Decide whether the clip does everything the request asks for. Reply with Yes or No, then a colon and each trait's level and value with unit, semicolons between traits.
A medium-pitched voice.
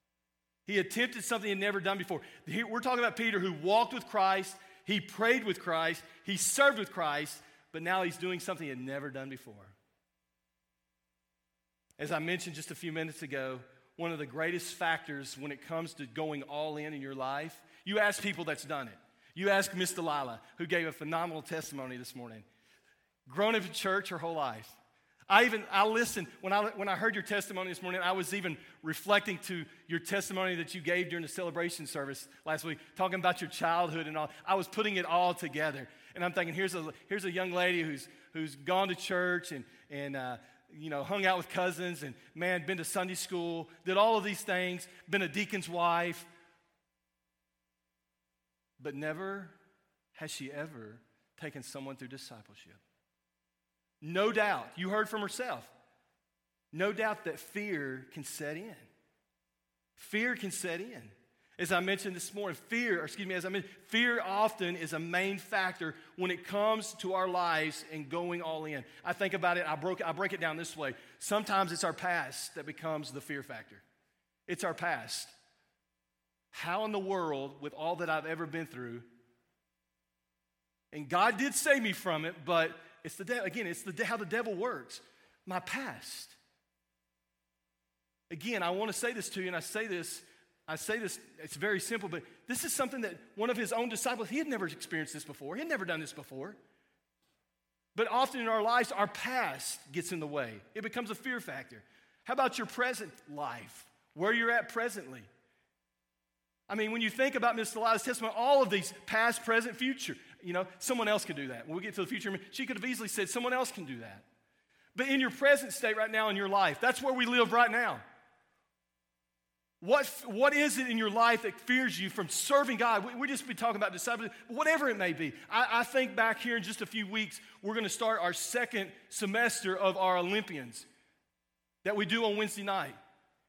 Yes: medium, 180 Hz